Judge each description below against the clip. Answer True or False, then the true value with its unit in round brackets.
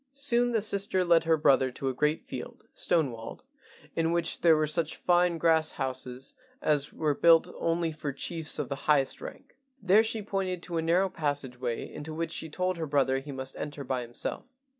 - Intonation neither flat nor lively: True (4.1 semitones)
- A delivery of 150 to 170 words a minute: False (195 wpm)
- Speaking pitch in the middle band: True (160 Hz)